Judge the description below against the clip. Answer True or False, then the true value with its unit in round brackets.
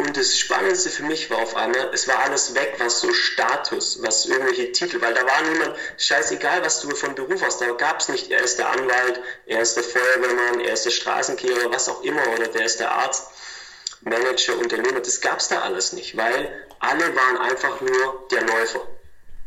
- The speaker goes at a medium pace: False (205 wpm)